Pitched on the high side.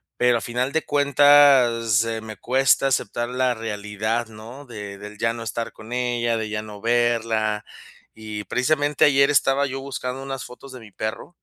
No: low, 120 Hz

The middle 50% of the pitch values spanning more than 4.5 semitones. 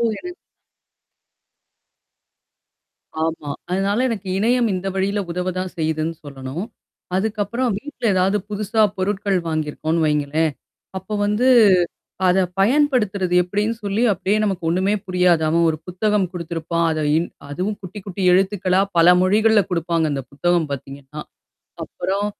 No: average, 3.8 semitones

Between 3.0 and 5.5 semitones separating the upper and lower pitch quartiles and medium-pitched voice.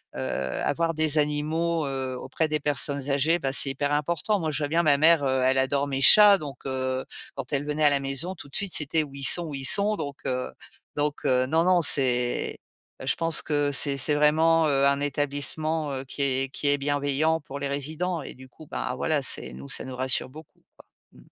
No: narrow, 2.6 semitones; medium, 145 Hz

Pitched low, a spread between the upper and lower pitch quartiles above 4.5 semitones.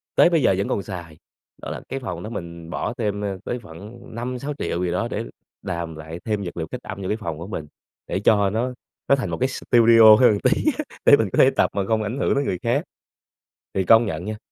Yes: low, 105 Hz; average, 5.3 semitones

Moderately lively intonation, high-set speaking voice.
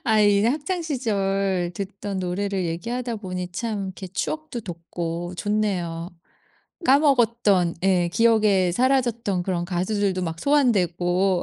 Yes: average, 4.5 semitones; high, 195 Hz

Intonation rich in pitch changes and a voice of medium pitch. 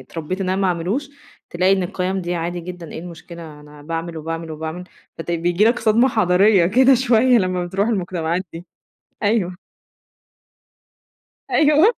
No: average, 3.7 semitones; medium, 180 Hz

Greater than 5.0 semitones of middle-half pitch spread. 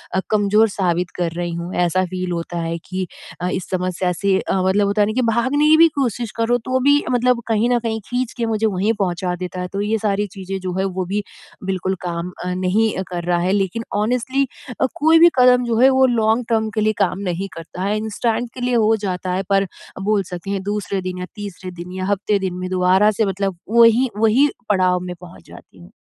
No: average, 3.8 semitones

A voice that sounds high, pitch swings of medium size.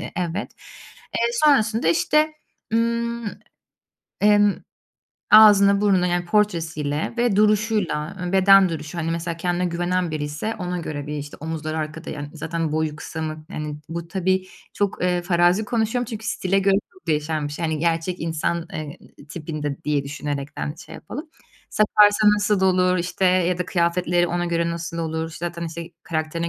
No: medium, 175 Hz; average, 3.9 semitones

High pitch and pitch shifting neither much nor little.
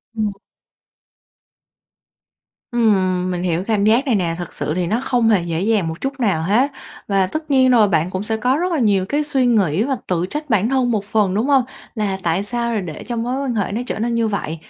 Yes: high, 215 Hz; average, 4.8 semitones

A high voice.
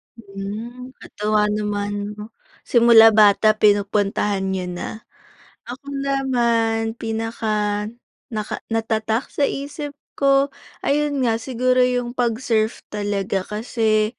Yes: high, 225 Hz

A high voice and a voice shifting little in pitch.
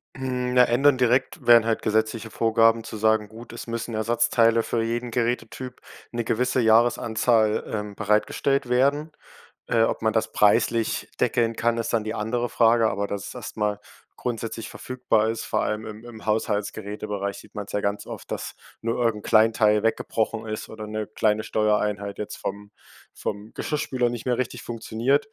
No: low, 115 Hz; narrow, 1.9 semitones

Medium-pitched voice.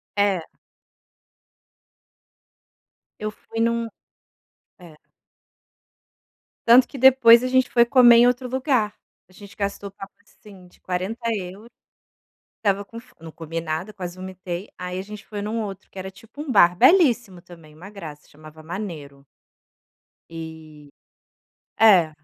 No: high, 200 Hz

